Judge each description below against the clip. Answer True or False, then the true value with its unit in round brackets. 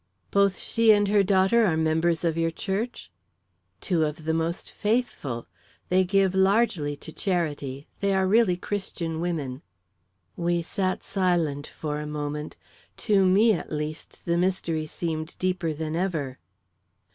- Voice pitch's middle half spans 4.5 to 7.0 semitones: False (3.7 semitones)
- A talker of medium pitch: True (170 Hz)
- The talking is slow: False (145 wpm)